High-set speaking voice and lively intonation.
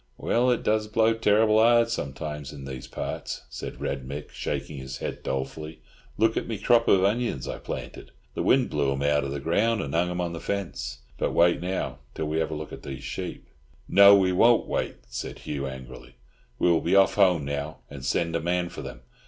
No: very low, 85 Hz; wide, 6.7 semitones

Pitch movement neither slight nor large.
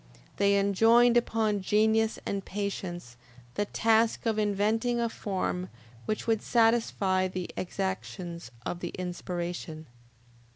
Yes: average, 3.3 semitones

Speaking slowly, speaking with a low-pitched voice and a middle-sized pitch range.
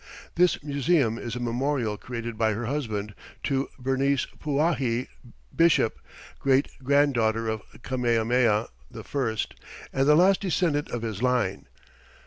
Yes: slow, 120 wpm; low, 125 Hz; average, 3.9 semitones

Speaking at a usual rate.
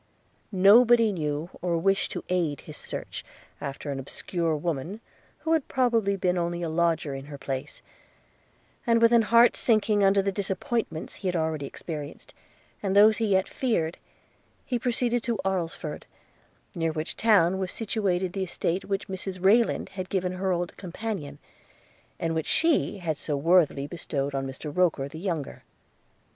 Yes: average, 160 wpm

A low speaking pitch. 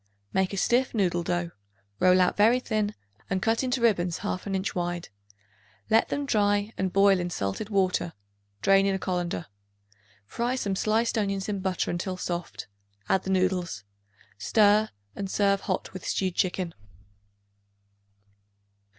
No: high, 195 Hz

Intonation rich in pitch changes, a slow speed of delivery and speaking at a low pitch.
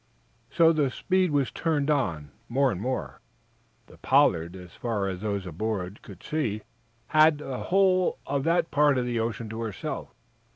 No: wide, 6.7 semitones; average, 165 wpm; low, 125 Hz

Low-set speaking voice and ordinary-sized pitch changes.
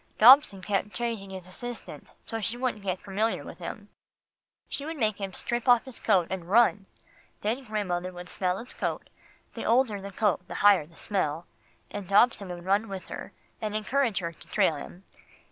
No: high, 205 Hz; average, 3.7 semitones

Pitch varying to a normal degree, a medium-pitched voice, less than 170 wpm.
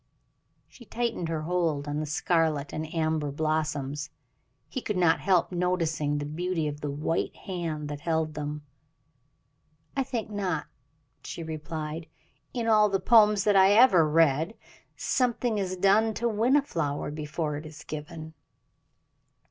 Yes: average, 4.7 semitones; medium, 165 Hz; average, 150 wpm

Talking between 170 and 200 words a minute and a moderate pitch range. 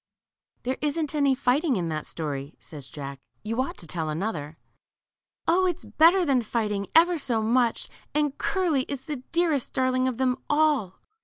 No: average, 175 wpm; wide, 7.4 semitones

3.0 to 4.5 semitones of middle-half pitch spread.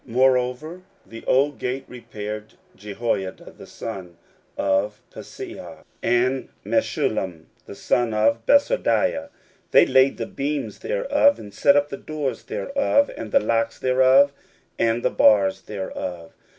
No: average, 4.9 semitones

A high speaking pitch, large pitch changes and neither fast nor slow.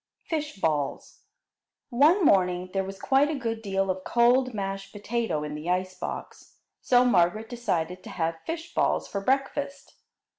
Yes: high, 200 Hz; wide, 5.7 semitones; average, 155 wpm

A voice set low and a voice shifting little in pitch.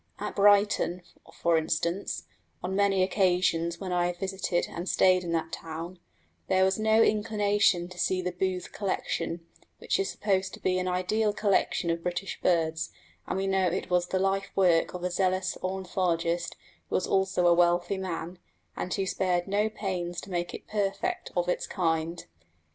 No: medium, 185 Hz; narrow, 1.9 semitones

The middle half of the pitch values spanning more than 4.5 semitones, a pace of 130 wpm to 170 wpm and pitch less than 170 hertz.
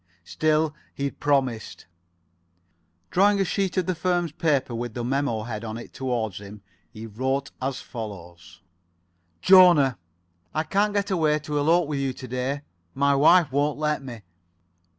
Yes: average, 5.0 semitones; average, 155 wpm; medium, 140 Hz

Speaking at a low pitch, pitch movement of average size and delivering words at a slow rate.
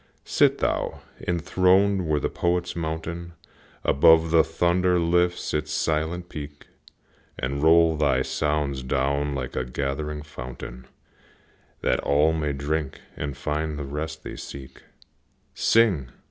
Yes: very low, 75 Hz; average, 3.0 semitones; slow, 125 wpm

